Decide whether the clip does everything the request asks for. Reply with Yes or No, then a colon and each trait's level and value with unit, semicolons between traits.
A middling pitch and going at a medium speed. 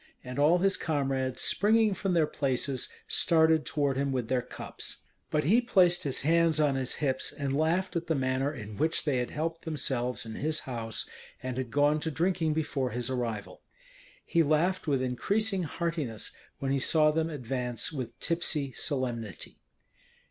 Yes: medium, 145 Hz; average, 170 wpm